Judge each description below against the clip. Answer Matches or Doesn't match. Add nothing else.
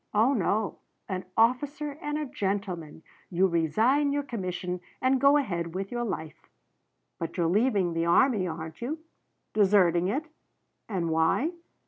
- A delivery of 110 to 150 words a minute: Matches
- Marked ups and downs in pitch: Matches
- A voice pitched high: Matches